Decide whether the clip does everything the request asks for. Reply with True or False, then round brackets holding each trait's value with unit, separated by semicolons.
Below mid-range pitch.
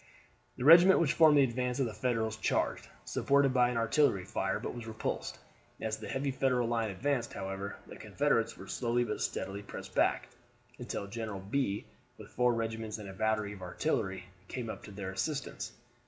True (115 Hz)